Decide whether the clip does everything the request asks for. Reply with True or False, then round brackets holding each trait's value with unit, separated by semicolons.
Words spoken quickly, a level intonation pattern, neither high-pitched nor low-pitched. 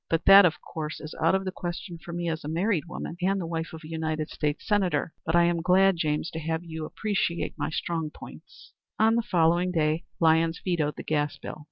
True (225 wpm; 2.2 semitones; 165 Hz)